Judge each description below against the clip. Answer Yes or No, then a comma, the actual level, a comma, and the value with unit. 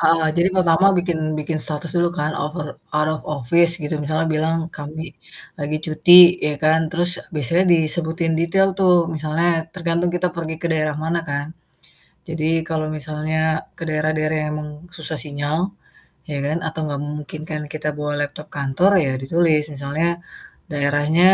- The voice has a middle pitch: Yes, medium, 155 Hz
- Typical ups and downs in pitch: No, narrow, 1.9 semitones